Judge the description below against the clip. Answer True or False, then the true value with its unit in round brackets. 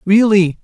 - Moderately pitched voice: False (195 Hz)